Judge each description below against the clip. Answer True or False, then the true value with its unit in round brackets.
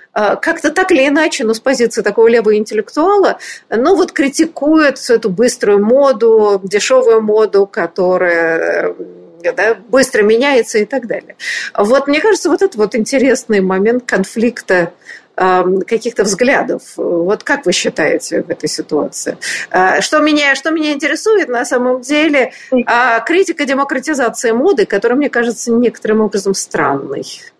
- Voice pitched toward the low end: False (235 Hz)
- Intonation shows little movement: False (5.1 semitones)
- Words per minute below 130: False (135 wpm)